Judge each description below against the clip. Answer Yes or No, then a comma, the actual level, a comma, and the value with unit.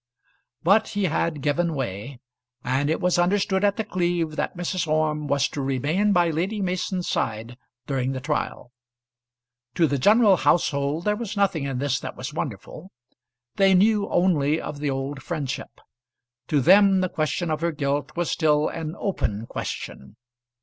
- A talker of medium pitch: Yes, medium, 155 Hz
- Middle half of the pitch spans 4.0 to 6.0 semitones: Yes, average, 4.8 semitones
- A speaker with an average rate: Yes, average, 165 wpm